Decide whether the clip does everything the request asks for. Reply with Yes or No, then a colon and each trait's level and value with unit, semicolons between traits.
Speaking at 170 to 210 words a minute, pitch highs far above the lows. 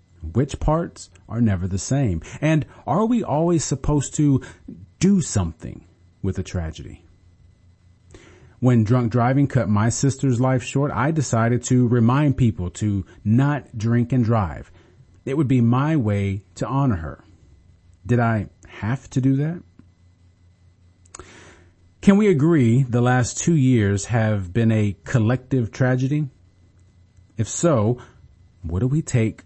No: slow, 135 wpm; wide, 6.3 semitones